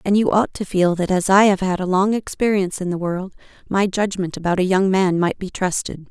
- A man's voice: No, female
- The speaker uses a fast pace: Yes, fast, 245 wpm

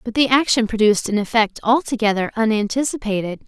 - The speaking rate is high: No, average, 140 wpm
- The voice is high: Yes, high, 225 Hz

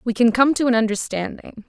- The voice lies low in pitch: No, high, 235 Hz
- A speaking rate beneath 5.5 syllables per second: No, 5.7 syllables/s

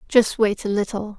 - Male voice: No, female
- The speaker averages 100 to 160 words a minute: No, average, 200 wpm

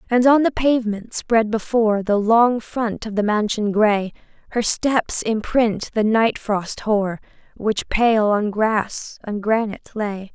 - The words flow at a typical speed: Yes, average, 155 wpm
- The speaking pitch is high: Yes, high, 220 Hz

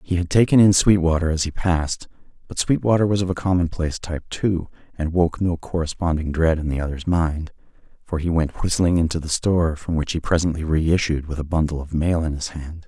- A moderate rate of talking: No, fast, 210 wpm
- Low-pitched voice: Yes, very low, 85 Hz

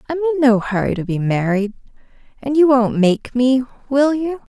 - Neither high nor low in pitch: No, high, 240 Hz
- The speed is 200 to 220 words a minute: No, average, 185 wpm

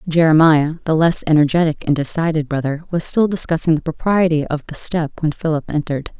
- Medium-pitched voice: Yes, medium, 160 Hz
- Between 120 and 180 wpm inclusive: Yes, average, 175 wpm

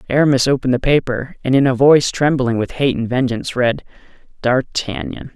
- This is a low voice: Yes, low, 130 Hz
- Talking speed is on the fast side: No, average, 170 wpm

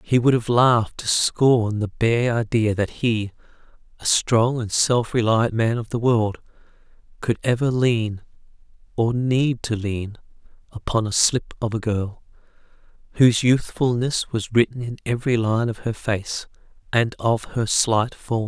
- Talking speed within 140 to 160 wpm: Yes, average, 155 wpm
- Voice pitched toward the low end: Yes, low, 115 Hz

